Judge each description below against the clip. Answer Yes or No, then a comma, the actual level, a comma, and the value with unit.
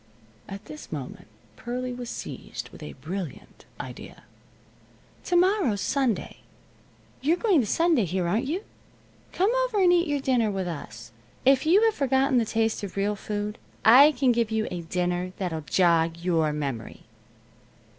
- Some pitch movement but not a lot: No, wide, 7.7 semitones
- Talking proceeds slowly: No, average, 155 wpm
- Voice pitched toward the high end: Yes, high, 220 Hz